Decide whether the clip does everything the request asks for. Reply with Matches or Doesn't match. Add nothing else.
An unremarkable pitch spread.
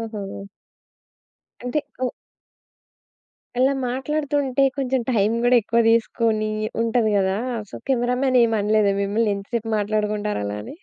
Matches